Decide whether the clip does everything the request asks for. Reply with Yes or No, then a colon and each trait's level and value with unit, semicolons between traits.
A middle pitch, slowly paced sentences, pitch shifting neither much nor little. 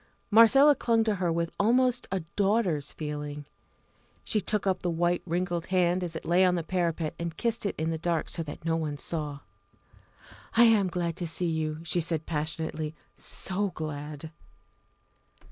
No: medium, 170 Hz; average, 175 wpm; average, 3.4 semitones